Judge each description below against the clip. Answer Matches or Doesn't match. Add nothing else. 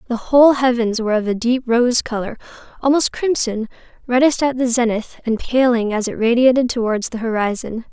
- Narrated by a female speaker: Matches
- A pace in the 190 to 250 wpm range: Doesn't match